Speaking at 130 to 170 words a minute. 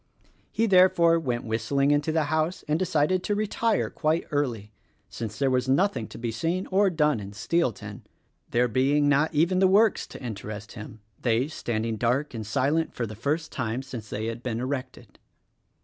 No: average, 185 wpm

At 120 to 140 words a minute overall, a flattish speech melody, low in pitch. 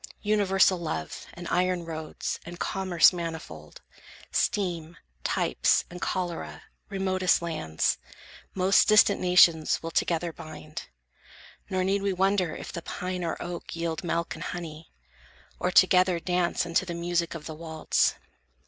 No: slow, 135 wpm; narrow, 2.0 semitones; medium, 175 Hz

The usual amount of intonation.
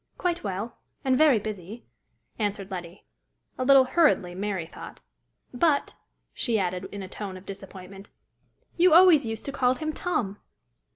No: wide, 6.2 semitones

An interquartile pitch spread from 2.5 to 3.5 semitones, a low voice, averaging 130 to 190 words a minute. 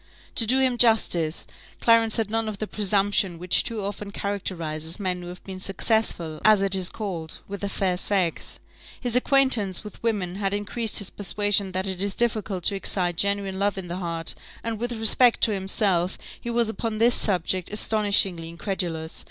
No: average, 3.2 semitones; high, 200 Hz; average, 180 wpm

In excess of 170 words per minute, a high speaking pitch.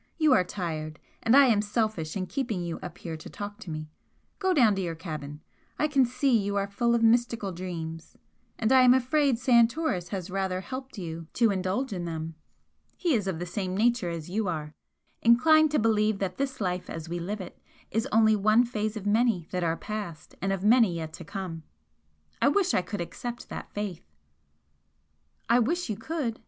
Yes: average, 200 wpm; high, 205 Hz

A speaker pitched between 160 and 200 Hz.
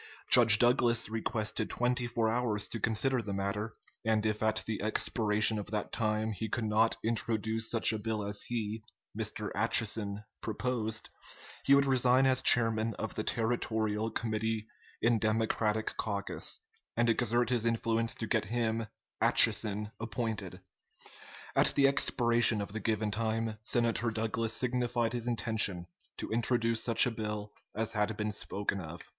No: low, 110 Hz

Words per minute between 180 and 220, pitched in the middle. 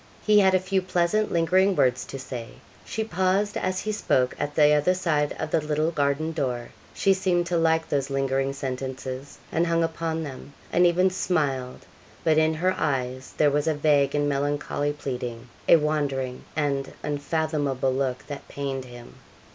No: average, 170 wpm; medium, 150 Hz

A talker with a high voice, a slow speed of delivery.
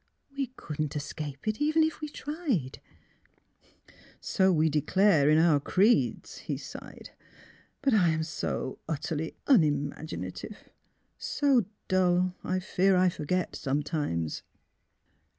No: medium, 170 Hz; slow, 130 wpm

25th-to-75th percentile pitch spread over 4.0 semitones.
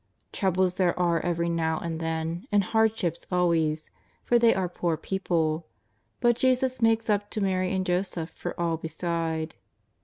No: average, 3.6 semitones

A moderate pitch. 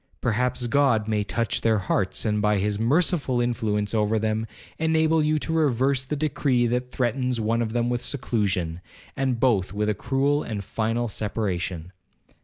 No: low, 115 Hz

